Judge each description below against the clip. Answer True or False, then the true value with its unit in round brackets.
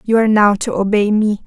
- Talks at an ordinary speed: False (245 wpm)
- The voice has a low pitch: False (210 Hz)